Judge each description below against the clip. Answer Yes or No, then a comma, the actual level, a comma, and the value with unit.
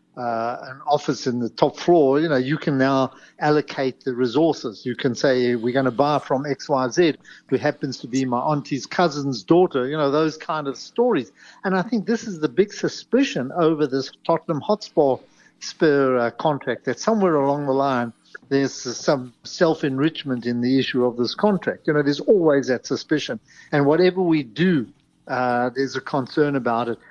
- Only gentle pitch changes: No, average, 3.7 semitones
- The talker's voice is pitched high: No, medium, 140 Hz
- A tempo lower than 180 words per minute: No, average, 185 wpm